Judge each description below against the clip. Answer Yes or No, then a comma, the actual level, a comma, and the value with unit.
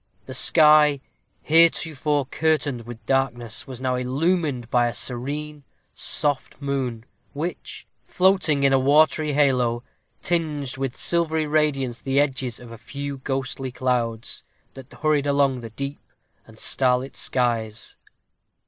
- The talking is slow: Yes, slow, 125 wpm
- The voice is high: No, low, 135 Hz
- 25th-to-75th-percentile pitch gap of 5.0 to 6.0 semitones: No, average, 3.2 semitones